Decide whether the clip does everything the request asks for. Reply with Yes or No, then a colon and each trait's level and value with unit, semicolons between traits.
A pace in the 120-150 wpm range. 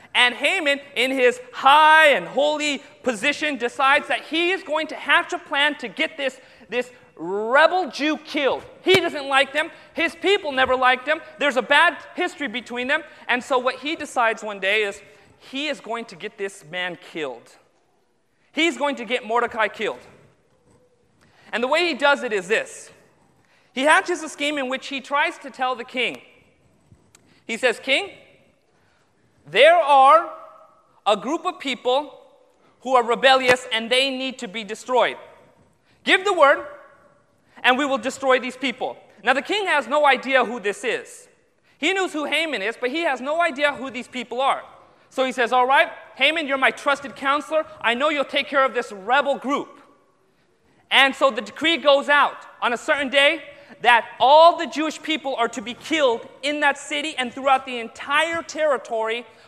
No: average, 180 wpm